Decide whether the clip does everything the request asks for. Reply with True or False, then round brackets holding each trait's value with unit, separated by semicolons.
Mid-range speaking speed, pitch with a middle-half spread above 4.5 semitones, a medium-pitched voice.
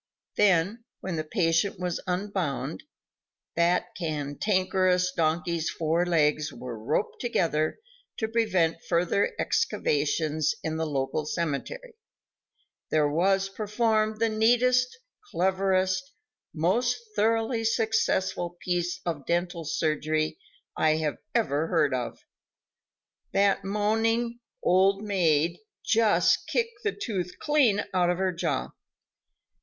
False (105 wpm; 5.1 semitones; 180 Hz)